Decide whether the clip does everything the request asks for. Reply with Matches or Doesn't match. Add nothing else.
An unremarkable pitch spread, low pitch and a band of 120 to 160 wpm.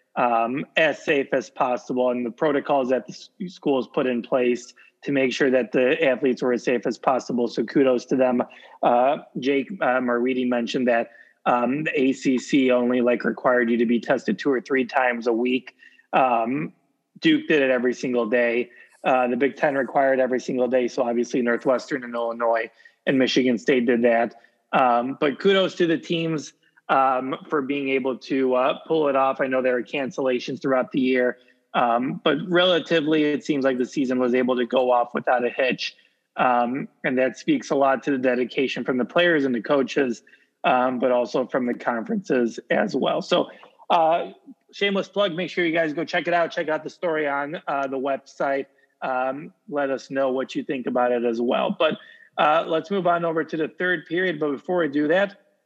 Doesn't match